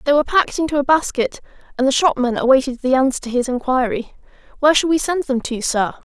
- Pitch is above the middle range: Yes, very high, 275 Hz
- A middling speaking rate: No, fast, 215 wpm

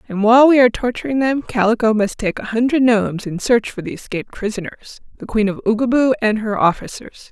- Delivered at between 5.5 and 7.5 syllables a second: Yes, 6.0 syllables/s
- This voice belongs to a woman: Yes, female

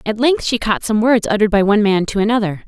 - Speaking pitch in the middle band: No, high, 215 Hz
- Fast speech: Yes, fast, 270 wpm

